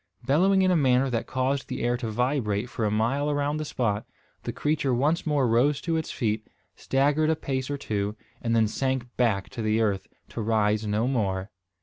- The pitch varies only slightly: No, average, 4.6 semitones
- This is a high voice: No, low, 125 Hz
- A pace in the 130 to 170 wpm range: No, fast, 205 wpm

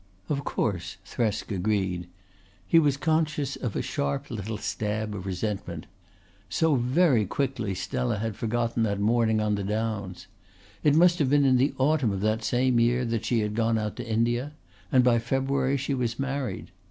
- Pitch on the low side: Yes, low, 115 Hz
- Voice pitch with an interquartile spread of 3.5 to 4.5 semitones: Yes, average, 4.1 semitones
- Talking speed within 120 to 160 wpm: No, average, 175 wpm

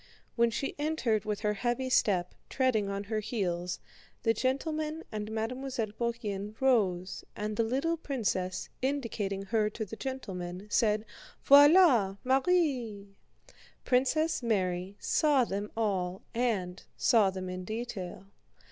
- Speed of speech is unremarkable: No, slow, 125 wpm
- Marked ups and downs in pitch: No, average, 4.7 semitones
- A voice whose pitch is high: Yes, high, 220 Hz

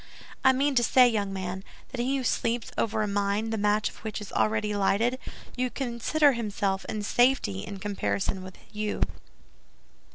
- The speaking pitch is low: No, high, 215 Hz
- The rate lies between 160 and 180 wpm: Yes, average, 170 wpm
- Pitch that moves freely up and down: No, average, 3.3 semitones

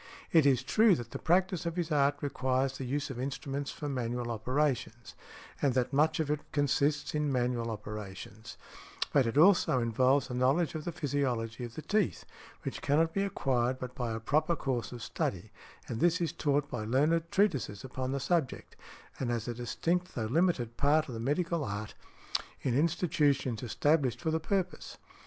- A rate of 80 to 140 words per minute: No, average, 180 wpm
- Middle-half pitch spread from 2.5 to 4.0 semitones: No, average, 4.4 semitones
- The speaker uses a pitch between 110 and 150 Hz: Yes, medium, 140 Hz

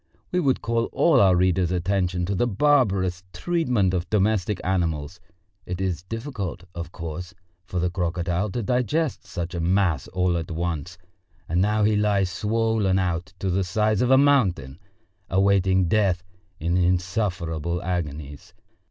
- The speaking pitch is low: Yes, very low, 95 Hz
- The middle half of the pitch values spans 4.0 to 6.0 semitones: No, average, 3.3 semitones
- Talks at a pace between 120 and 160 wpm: Yes, average, 145 wpm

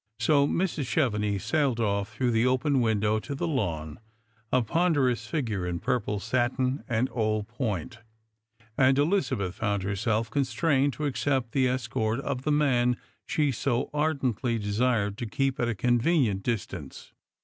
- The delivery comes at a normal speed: Yes, average, 150 wpm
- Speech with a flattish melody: No, average, 4.2 semitones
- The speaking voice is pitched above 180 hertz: No, low, 120 Hz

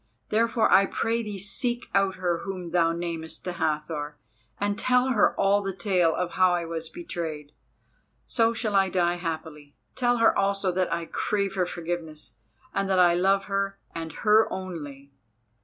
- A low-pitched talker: No, medium, 185 Hz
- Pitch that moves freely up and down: No, average, 3.3 semitones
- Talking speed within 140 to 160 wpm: No, average, 170 wpm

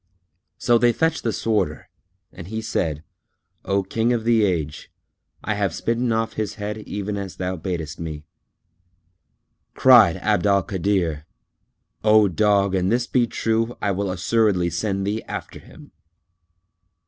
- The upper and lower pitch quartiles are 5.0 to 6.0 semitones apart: No, average, 3.5 semitones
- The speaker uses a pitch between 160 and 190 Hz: No, low, 100 Hz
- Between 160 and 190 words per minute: No, average, 145 wpm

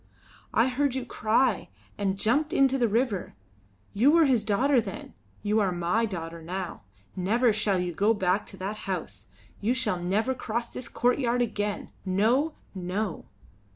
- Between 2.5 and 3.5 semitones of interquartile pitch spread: No, average, 4.6 semitones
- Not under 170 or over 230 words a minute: No, average, 155 wpm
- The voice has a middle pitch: No, high, 215 Hz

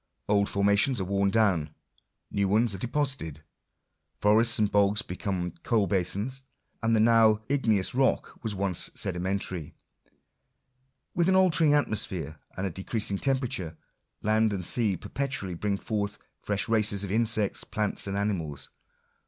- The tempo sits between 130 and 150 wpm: Yes, slow, 135 wpm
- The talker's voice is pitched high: No, low, 105 Hz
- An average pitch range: Yes, average, 3.1 semitones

